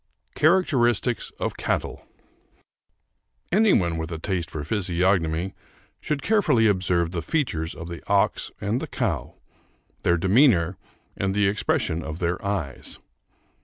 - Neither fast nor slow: No, slow, 130 wpm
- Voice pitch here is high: No, very low, 95 Hz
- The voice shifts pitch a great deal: Yes, wide, 5.8 semitones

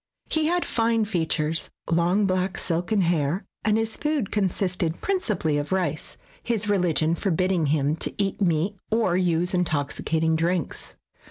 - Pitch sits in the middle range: Yes, medium, 180 Hz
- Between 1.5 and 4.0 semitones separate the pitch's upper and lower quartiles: No, average, 4.4 semitones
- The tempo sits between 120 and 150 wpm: Yes, average, 145 wpm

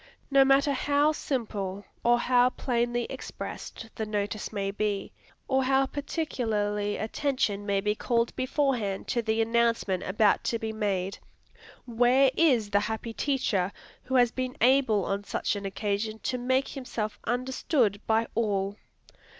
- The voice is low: No, high, 230 Hz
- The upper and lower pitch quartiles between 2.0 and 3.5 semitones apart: No, average, 4.0 semitones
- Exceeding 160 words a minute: No, average, 140 wpm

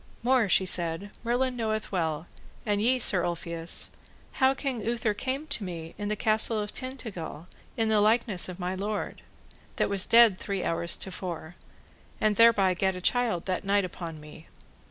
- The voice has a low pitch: No, high, 205 Hz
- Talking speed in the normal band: Yes, average, 175 wpm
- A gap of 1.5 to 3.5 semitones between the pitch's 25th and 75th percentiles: No, average, 4.5 semitones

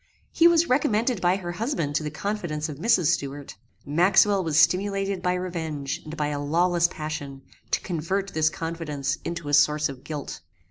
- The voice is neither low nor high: Yes, medium, 165 Hz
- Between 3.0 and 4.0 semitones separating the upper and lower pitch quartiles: No, average, 4.4 semitones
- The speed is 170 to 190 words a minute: Yes, average, 175 wpm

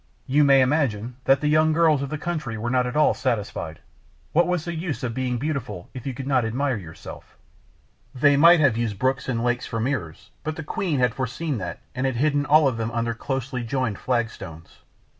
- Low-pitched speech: Yes, low, 130 Hz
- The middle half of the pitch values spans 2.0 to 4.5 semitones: Yes, average, 4.1 semitones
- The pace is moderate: No, fast, 215 wpm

